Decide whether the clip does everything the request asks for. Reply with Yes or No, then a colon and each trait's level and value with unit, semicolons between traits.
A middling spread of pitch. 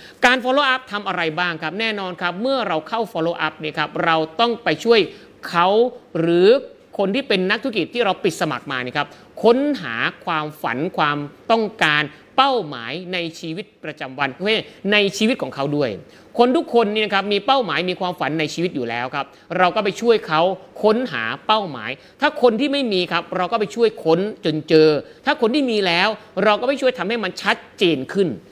No: wide, 6.4 semitones